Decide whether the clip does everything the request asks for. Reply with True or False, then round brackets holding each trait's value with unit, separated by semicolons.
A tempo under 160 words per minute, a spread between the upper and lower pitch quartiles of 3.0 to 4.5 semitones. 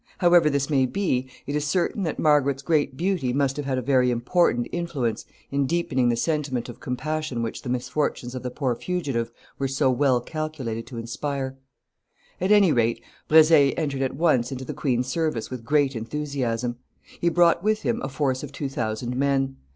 False (185 wpm; 3.7 semitones)